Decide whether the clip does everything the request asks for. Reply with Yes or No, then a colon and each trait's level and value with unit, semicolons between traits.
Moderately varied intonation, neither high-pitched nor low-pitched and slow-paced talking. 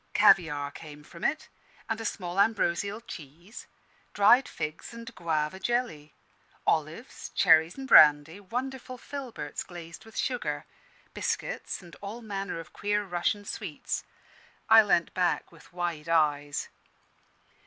No: wide, 6.0 semitones; medium, 180 Hz; slow, 125 wpm